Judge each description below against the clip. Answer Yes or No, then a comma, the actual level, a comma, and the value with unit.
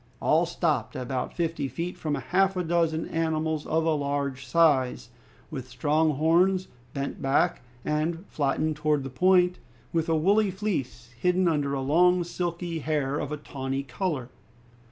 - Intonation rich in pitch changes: No, average, 3.8 semitones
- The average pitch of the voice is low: No, medium, 155 Hz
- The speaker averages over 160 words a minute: No, average, 150 wpm